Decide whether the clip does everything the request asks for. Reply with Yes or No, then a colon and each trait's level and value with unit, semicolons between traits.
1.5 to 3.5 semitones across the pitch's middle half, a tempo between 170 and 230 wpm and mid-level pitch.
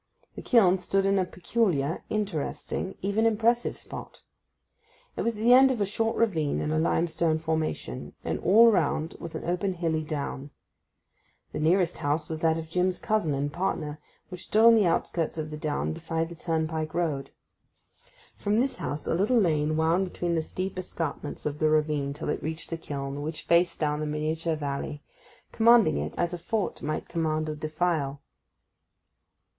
No: average, 3.9 semitones; average, 175 wpm; medium, 165 Hz